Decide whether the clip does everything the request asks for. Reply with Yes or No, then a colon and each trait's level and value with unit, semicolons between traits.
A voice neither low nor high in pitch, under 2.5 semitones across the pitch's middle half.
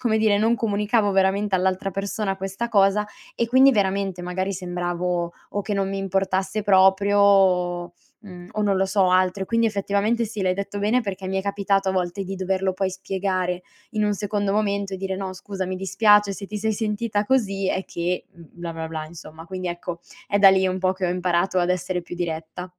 No: high, 195 Hz; narrow, 1.9 semitones